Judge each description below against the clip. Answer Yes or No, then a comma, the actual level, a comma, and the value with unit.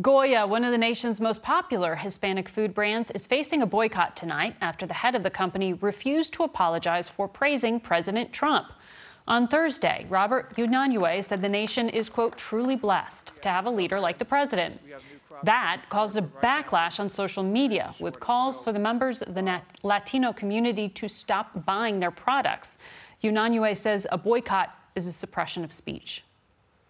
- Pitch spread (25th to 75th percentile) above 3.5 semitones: Yes, average, 4.2 semitones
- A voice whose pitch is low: No, high, 215 Hz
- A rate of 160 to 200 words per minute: Yes, average, 170 wpm